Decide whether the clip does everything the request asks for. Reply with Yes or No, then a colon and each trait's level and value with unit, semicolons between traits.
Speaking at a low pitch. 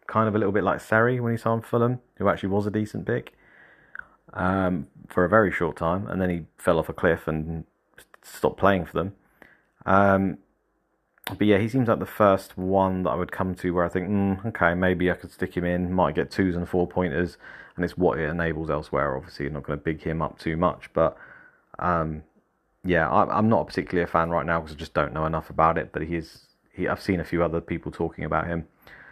Yes: very low, 90 Hz